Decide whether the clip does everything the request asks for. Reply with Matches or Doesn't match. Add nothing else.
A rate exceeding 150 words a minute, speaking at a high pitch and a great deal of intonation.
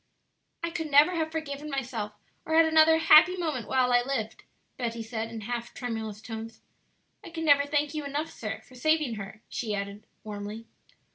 Matches